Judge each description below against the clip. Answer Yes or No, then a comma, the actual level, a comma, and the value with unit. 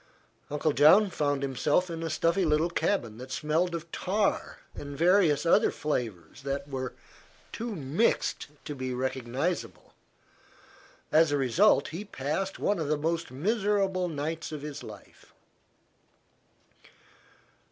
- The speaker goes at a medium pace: No, slow, 130 wpm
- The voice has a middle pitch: Yes, medium, 155 Hz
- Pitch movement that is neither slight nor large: Yes, average, 4.5 semitones